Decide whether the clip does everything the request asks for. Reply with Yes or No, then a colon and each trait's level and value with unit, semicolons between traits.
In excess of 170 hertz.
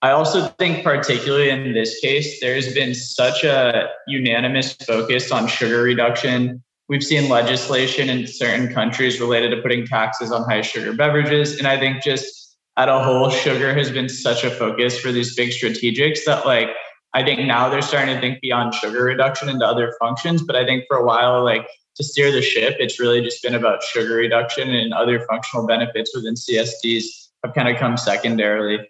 No: low, 125 Hz